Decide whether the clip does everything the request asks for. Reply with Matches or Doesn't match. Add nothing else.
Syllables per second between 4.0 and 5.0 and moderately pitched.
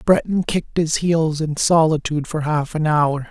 Matches